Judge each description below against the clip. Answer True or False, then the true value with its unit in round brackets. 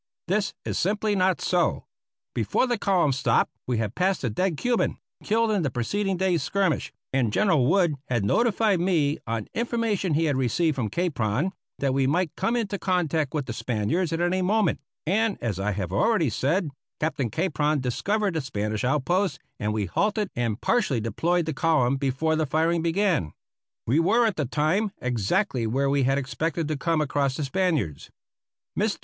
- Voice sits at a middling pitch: True (160 Hz)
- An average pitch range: False (6.6 semitones)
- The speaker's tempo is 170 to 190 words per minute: True (180 wpm)